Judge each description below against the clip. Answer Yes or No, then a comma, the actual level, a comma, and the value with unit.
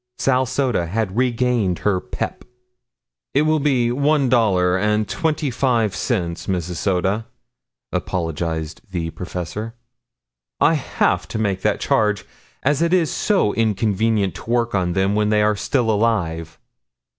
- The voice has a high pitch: No, low, 105 Hz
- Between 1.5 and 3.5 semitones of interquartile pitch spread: No, average, 5.1 semitones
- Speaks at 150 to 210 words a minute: No, average, 140 wpm